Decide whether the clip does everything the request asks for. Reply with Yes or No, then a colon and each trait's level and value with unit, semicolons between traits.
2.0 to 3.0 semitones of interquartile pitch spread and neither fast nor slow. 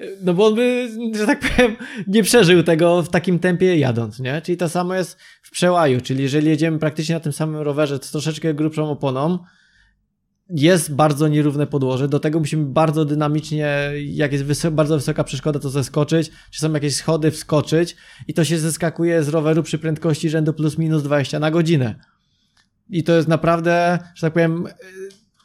No: narrow, 2.4 semitones; fast, 180 wpm